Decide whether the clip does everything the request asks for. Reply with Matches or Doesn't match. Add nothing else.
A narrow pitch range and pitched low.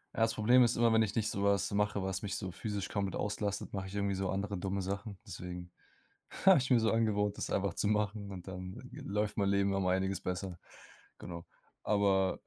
Matches